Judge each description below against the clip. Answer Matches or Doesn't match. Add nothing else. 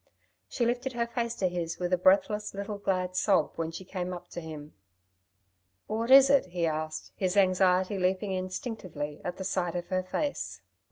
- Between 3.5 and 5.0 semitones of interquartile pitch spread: Doesn't match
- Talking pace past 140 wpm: Matches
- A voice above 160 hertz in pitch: Matches